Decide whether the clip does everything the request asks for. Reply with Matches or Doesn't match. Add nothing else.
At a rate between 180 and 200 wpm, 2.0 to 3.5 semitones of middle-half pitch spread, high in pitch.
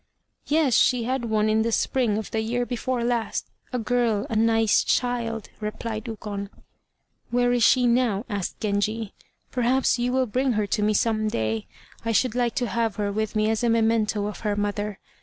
Matches